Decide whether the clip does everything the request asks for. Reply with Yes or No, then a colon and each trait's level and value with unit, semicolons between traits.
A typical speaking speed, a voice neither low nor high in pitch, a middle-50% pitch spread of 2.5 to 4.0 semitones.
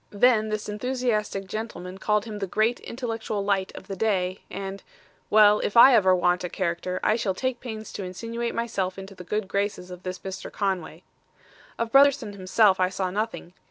No: average, 185 wpm; high, 205 Hz; average, 3.0 semitones